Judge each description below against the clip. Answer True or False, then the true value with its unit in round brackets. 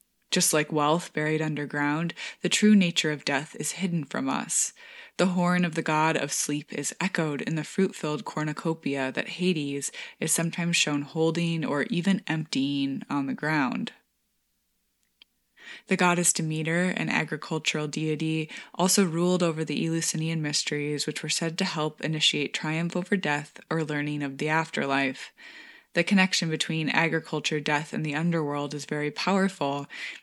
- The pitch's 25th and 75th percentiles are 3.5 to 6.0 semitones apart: False (3.0 semitones)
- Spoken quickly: False (155 wpm)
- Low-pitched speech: False (160 Hz)